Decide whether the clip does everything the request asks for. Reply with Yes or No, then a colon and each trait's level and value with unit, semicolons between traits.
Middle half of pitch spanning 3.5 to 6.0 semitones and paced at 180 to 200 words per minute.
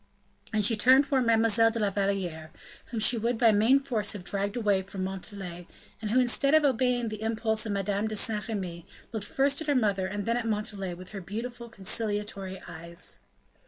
No: average, 3.1 semitones; average, 195 wpm